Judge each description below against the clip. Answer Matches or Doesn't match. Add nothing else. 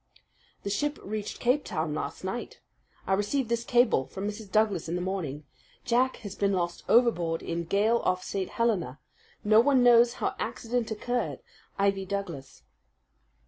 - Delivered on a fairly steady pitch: Doesn't match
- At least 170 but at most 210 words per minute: Doesn't match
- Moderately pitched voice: Doesn't match